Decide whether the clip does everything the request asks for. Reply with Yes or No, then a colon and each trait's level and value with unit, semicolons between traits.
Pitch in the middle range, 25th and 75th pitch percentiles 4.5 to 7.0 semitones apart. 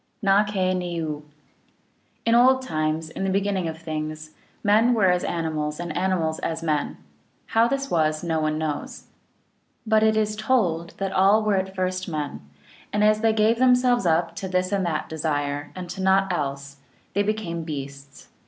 Yes: medium, 180 Hz; average, 5.1 semitones